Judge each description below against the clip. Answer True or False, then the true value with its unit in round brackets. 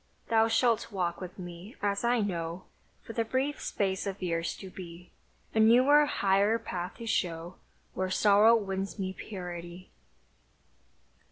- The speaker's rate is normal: True (145 wpm)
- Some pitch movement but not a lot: True (3.9 semitones)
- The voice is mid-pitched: False (195 Hz)